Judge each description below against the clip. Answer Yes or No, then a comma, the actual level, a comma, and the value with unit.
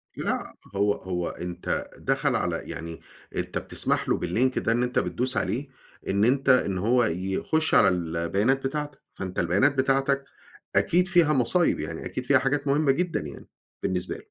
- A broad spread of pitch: Yes, wide, 6.8 semitones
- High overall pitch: No, low, 125 Hz